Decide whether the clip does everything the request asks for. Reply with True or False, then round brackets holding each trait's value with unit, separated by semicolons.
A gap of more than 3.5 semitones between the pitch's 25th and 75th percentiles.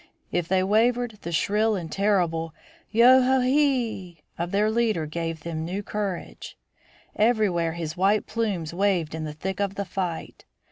True (4.5 semitones)